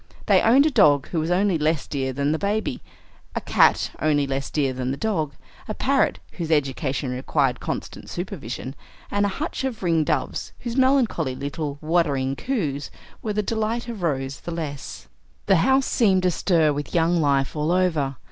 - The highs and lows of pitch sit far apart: Yes, wide, 6.1 semitones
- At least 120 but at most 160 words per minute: No, average, 175 wpm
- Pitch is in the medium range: Yes, medium, 160 Hz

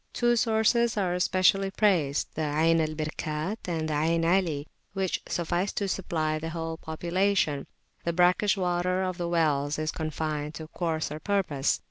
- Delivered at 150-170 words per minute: Yes, average, 155 wpm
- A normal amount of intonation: Yes, average, 3.3 semitones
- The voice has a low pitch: No, medium, 170 Hz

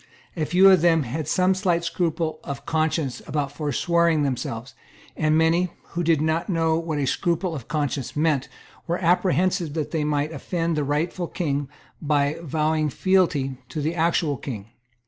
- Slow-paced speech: No, average, 165 wpm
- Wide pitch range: No, average, 2.7 semitones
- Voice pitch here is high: No, medium, 160 Hz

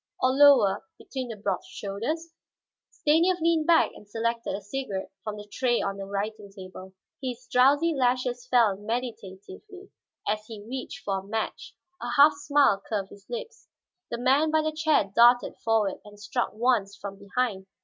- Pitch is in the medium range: No, high, 235 Hz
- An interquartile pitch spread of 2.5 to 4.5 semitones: No, wide, 5.6 semitones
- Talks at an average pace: Yes, average, 165 wpm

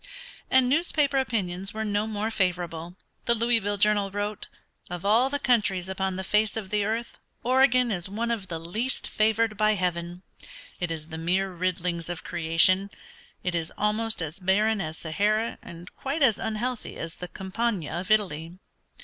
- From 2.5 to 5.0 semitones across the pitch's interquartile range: Yes, average, 3.9 semitones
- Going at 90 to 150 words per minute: No, average, 165 wpm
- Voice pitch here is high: Yes, high, 200 Hz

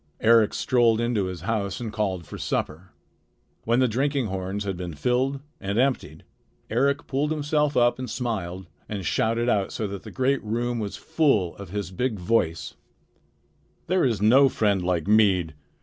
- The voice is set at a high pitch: No, low, 110 Hz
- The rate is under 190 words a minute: Yes, average, 165 wpm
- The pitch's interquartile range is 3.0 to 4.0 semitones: No, average, 4.9 semitones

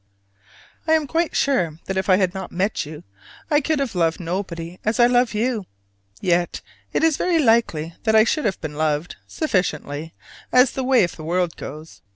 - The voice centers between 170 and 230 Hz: Yes, high, 190 Hz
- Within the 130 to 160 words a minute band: No, average, 190 wpm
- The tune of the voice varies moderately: No, wide, 7.2 semitones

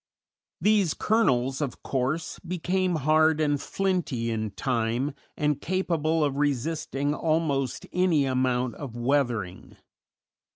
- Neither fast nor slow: No, slow, 110 wpm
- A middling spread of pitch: Yes, average, 4.2 semitones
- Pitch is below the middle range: No, medium, 145 Hz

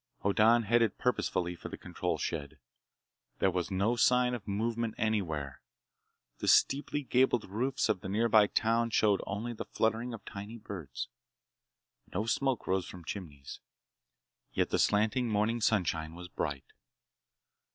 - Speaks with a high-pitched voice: No, low, 105 Hz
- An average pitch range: Yes, average, 4.1 semitones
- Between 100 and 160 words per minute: Yes, average, 140 wpm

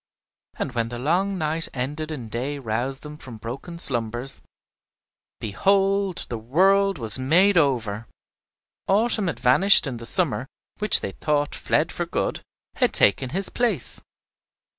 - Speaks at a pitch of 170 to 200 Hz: No, medium, 145 Hz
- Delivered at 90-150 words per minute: Yes, average, 140 wpm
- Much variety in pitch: Yes, wide, 7.6 semitones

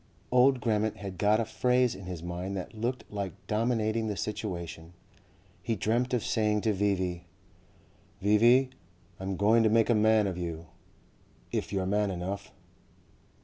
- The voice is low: Yes, low, 105 Hz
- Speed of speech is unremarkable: Yes, average, 150 wpm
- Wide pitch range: No, average, 3.1 semitones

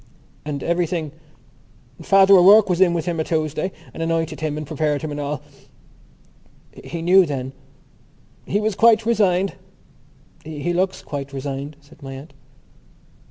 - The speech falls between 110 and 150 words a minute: Yes, average, 145 wpm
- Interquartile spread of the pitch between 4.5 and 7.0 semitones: No, average, 4.0 semitones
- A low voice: No, medium, 165 Hz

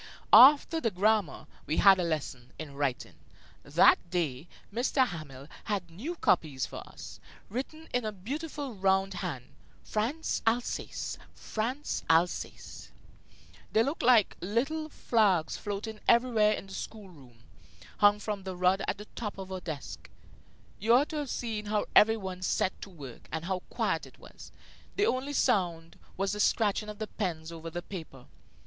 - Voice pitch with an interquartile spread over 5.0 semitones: Yes, wide, 5.4 semitones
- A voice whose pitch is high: Yes, high, 200 Hz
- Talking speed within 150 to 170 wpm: Yes, average, 160 wpm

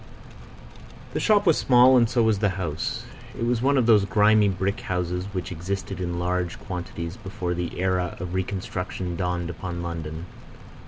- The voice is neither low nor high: No, very low, 95 Hz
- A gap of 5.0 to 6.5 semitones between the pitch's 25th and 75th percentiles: No, average, 3.3 semitones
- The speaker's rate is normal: Yes, average, 165 wpm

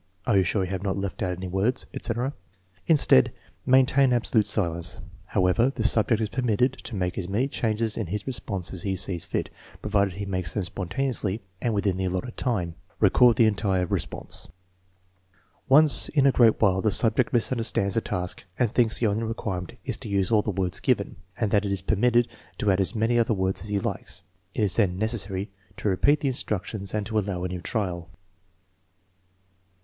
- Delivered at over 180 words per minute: Yes, average, 200 wpm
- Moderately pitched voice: No, low, 105 Hz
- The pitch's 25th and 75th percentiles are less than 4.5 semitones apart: Yes, average, 3.7 semitones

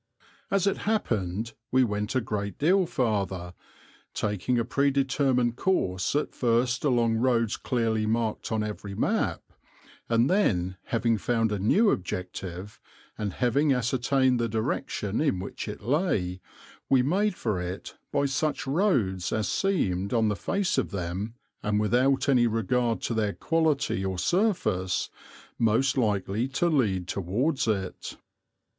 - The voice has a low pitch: Yes, low, 115 Hz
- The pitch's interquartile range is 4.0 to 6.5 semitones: Yes, average, 5.1 semitones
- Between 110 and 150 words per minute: Yes, average, 140 wpm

